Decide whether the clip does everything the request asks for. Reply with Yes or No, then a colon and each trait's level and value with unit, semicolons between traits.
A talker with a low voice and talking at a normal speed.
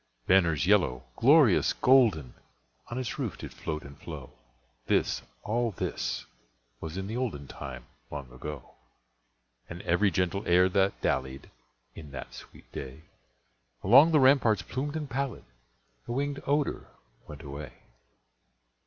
No: very low, 90 Hz; slow, 125 wpm